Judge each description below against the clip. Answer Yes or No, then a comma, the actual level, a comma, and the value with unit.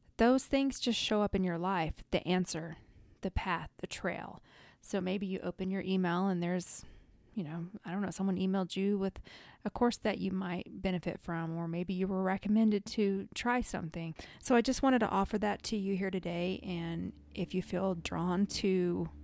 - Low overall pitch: No, high, 190 Hz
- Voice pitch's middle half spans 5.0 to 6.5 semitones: No, narrow, 2.4 semitones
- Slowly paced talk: No, average, 195 wpm